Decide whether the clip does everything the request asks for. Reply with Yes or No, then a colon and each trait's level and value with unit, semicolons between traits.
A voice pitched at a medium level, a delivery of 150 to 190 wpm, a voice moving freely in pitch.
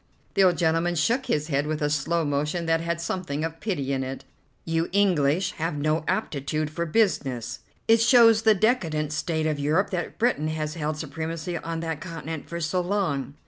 No: medium, 160 Hz; average, 185 wpm; average, 2.9 semitones